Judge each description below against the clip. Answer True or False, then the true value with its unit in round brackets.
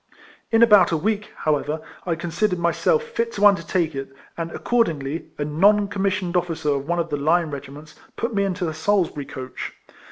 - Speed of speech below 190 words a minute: True (180 wpm)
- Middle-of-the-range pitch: True (170 Hz)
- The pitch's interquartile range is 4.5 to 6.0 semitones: True (4.9 semitones)